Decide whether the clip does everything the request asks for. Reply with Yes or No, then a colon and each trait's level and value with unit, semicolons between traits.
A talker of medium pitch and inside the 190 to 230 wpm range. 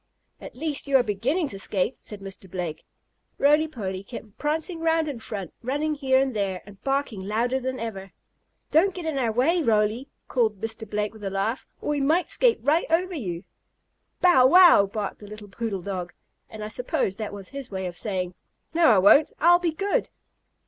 No: high, 235 Hz; average, 195 wpm